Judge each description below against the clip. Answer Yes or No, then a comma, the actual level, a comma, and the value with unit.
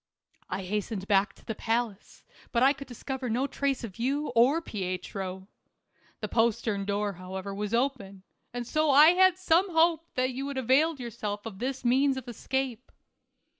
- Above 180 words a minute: No, average, 170 wpm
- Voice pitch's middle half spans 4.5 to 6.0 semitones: Yes, average, 5.2 semitones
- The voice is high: Yes, high, 240 Hz